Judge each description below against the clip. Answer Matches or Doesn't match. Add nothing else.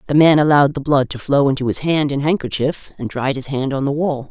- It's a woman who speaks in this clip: Matches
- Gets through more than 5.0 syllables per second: Matches